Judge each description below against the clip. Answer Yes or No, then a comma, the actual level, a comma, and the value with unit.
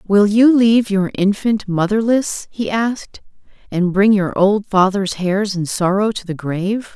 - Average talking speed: Yes, average, 165 wpm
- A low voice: No, high, 200 Hz